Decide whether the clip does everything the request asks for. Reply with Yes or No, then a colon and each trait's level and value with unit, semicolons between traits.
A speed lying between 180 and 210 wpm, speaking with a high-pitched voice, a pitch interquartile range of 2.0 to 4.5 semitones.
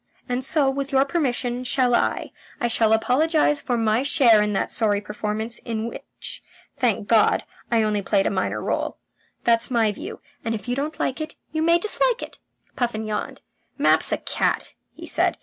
Yes: average, 185 wpm; high, 240 Hz; average, 4.0 semitones